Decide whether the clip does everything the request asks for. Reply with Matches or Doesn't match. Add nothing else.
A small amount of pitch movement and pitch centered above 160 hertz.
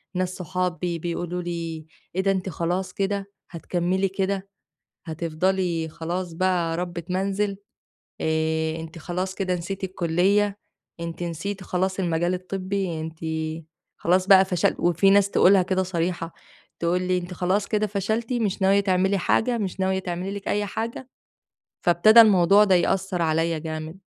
Matches